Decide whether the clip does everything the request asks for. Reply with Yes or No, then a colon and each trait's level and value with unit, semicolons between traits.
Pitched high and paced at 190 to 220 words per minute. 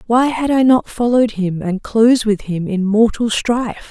Yes: high, 225 Hz; average, 200 wpm